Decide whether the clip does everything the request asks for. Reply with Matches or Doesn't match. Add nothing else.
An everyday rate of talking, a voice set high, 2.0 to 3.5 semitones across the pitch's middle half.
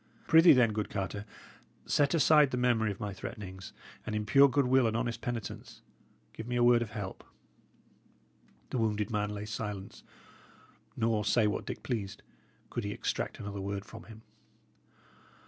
Doesn't match